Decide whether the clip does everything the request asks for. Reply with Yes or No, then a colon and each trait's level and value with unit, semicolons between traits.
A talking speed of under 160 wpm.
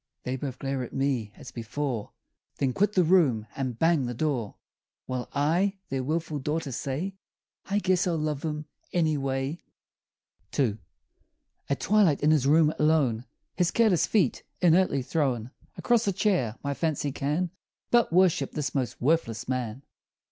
Yes: average, 150 wpm